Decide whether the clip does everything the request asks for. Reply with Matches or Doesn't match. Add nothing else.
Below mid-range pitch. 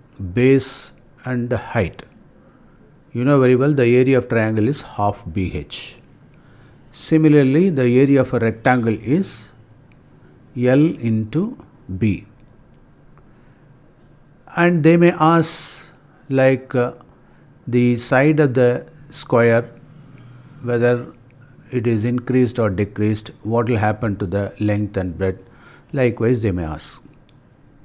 Matches